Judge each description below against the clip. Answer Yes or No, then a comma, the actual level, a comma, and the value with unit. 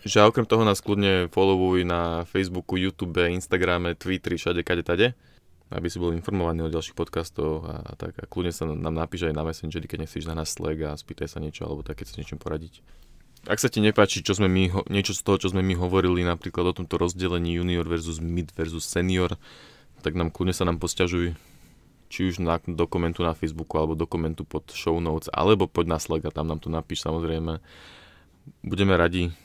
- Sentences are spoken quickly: Yes, fast, 205 wpm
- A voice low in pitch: Yes, very low, 85 Hz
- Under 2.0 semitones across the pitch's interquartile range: No, narrow, 2.4 semitones